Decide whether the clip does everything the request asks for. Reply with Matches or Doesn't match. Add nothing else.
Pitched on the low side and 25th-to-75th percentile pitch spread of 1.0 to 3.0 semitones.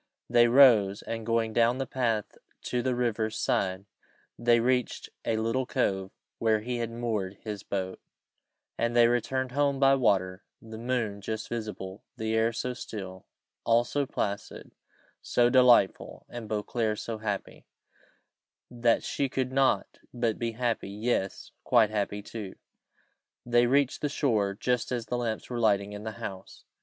Matches